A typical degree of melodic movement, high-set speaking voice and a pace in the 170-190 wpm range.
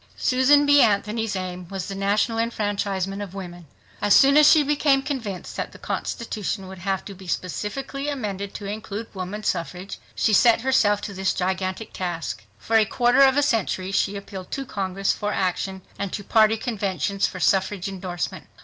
Yes: average, 3.2 semitones; high, 200 Hz; average, 175 wpm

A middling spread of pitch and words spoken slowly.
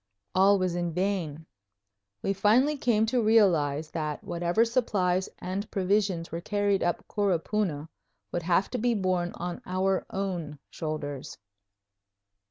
Yes: average, 3.3 semitones; slow, 130 wpm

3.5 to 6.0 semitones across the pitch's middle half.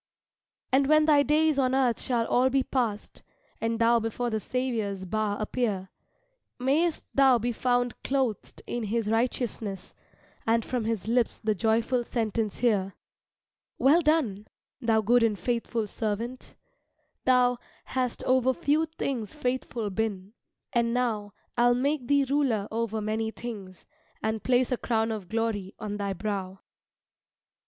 No: average, 3.0 semitones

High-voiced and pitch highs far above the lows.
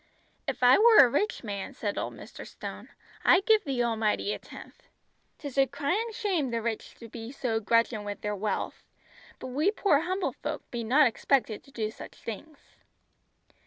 Yes: very high, 250 Hz; wide, 5.7 semitones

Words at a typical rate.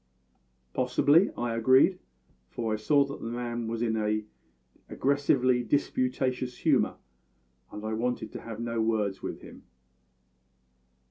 No: slow, 130 wpm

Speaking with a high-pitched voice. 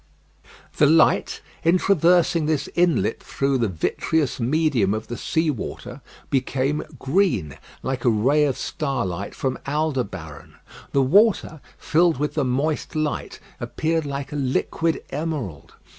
No: medium, 145 Hz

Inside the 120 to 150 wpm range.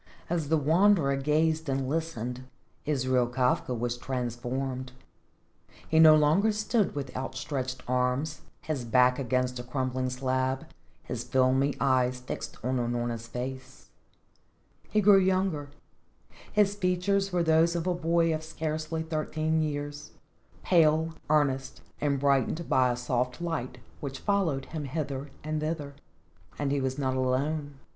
Yes: slow, 135 wpm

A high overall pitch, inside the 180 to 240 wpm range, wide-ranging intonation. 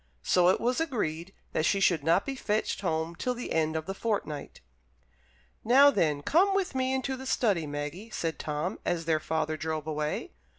No: medium, 175 Hz; average, 185 wpm; wide, 7.8 semitones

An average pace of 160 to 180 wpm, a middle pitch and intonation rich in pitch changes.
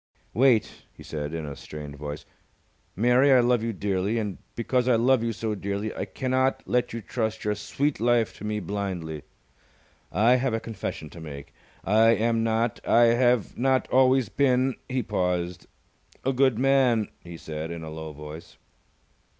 No: average, 170 wpm; low, 110 Hz; wide, 5.9 semitones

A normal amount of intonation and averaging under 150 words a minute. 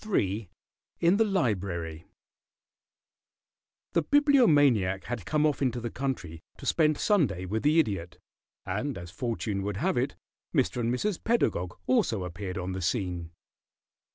No: wide, 8.6 semitones; average, 140 wpm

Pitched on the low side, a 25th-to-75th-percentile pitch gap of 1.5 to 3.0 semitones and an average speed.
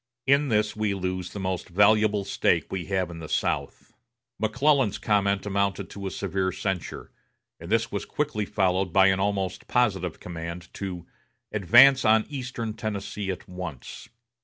Yes: low, 100 Hz; average, 2.7 semitones; average, 155 wpm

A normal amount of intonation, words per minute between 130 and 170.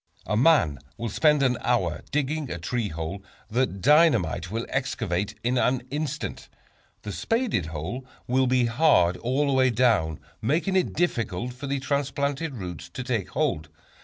No: wide, 6.2 semitones; average, 160 wpm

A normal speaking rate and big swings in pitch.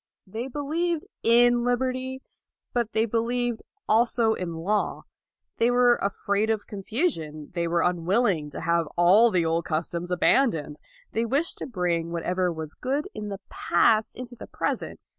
Yes: average, 155 wpm; wide, 6.0 semitones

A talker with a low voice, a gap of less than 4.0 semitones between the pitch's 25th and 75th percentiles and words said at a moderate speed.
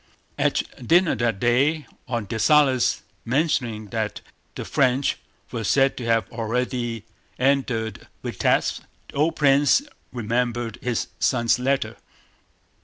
No: low, 125 Hz; average, 3.1 semitones; slow, 110 wpm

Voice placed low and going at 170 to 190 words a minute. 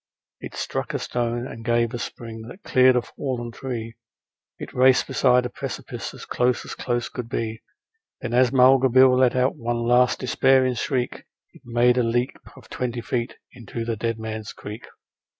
Yes: low, 120 Hz; average, 185 wpm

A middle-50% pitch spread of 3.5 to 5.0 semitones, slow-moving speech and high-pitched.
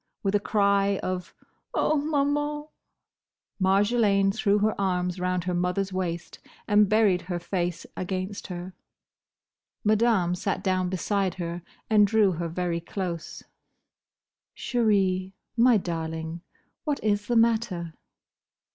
No: average, 3.0 semitones; slow, 115 wpm; high, 195 Hz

